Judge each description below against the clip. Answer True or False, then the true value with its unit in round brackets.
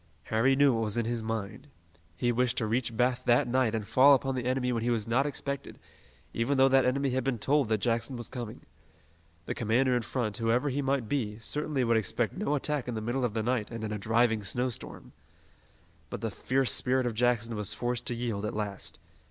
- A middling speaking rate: False (220 wpm)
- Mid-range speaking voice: False (120 Hz)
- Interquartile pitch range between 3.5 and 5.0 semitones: False (2.7 semitones)